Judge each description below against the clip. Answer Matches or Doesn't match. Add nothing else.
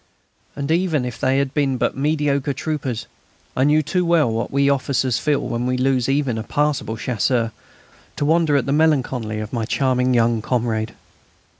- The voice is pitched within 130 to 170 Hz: Matches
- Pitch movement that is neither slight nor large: Matches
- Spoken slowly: Doesn't match